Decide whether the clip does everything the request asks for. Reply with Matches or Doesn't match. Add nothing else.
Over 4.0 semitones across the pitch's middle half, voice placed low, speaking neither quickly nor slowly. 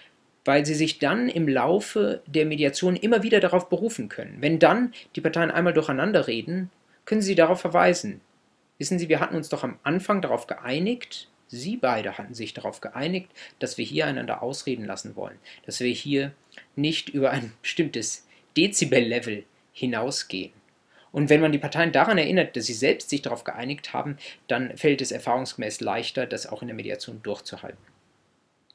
Doesn't match